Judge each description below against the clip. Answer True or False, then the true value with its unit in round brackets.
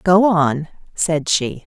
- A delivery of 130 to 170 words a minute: True (135 wpm)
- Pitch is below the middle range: False (165 Hz)